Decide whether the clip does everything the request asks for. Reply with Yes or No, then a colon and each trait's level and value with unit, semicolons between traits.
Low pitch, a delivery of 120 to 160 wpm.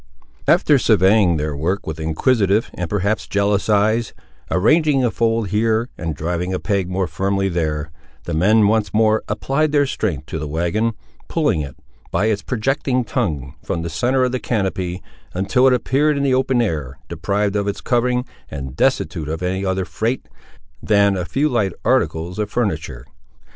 No: low, 100 Hz; average, 170 wpm